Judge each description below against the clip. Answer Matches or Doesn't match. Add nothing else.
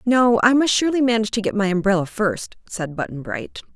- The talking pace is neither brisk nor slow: Doesn't match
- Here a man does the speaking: Doesn't match